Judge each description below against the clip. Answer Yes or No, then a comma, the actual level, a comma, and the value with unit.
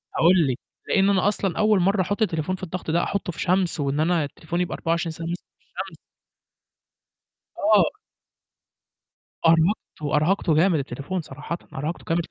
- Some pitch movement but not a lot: Yes, average, 3.0 semitones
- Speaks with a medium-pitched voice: Yes, medium, 170 Hz